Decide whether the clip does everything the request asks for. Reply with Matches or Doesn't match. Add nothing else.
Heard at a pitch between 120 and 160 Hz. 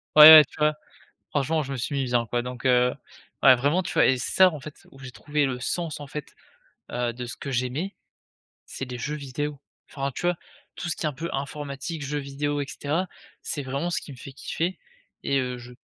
Matches